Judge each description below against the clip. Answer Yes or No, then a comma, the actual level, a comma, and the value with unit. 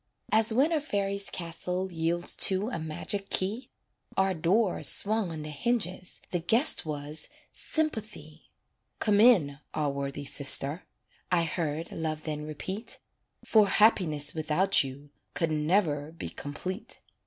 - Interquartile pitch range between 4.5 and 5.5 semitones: Yes, average, 5.0 semitones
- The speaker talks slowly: Yes, slow, 130 wpm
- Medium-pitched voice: Yes, medium, 175 Hz